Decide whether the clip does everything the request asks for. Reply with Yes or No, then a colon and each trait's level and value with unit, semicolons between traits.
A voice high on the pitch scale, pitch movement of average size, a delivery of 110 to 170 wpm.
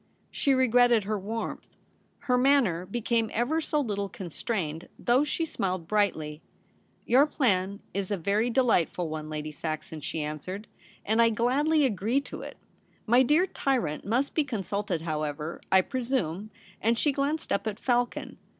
No: high, 215 Hz; wide, 6.2 semitones; average, 160 wpm